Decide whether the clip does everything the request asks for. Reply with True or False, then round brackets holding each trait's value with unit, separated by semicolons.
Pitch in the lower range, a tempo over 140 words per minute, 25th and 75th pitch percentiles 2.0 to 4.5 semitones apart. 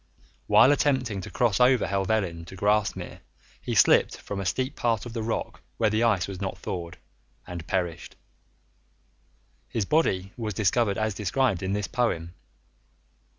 True (105 Hz; 150 wpm; 3.9 semitones)